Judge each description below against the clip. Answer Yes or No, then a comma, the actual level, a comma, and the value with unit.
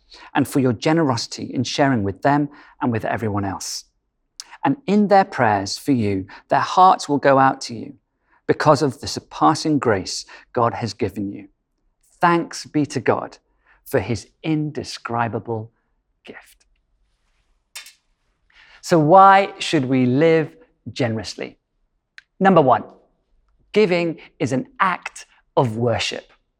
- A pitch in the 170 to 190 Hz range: No, low, 135 Hz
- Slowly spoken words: Yes, slow, 125 wpm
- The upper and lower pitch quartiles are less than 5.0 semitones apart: No, average, 5.3 semitones